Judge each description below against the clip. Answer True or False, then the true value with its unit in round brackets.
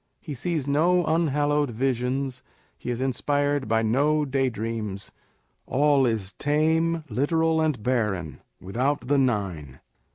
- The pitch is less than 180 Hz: True (135 Hz)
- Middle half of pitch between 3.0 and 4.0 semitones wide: False (4.6 semitones)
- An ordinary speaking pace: False (120 wpm)